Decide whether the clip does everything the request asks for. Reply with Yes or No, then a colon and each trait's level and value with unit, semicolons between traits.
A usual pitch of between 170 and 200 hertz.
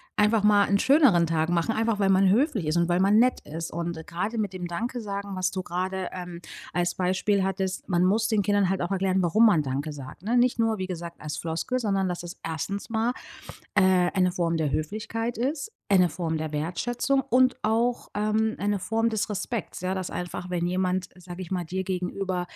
Yes: high, 190 Hz